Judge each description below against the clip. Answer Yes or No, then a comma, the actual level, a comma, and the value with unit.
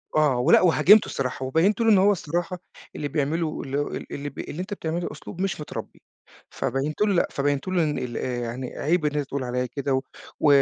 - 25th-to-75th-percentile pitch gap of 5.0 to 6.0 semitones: No, average, 4.4 semitones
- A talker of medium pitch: Yes, medium, 150 Hz